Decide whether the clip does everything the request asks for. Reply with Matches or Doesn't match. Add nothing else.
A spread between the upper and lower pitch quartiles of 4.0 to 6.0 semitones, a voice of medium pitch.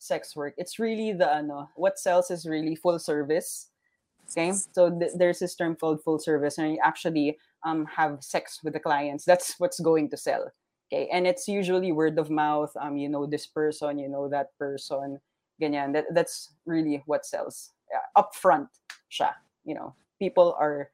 Doesn't match